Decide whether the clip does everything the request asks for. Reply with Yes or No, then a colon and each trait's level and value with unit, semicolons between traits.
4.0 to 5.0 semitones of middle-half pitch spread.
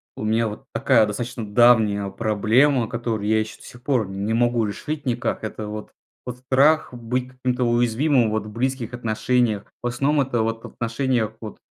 No: narrow, 2.6 semitones